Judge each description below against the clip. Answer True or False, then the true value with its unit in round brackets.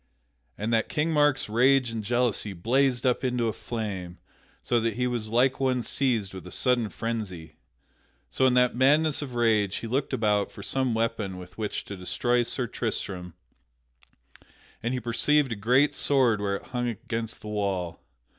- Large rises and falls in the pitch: False (3.5 semitones)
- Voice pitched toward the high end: False (115 Hz)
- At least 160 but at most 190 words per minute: True (175 wpm)